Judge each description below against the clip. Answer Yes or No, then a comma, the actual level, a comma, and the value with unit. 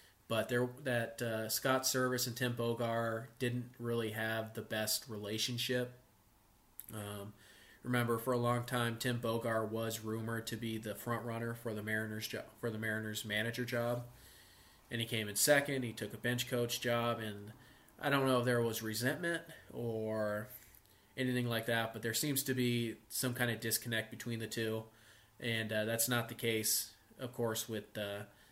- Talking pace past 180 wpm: No, average, 175 wpm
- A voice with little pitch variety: Yes, narrow, 1.9 semitones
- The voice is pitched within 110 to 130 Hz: Yes, low, 115 Hz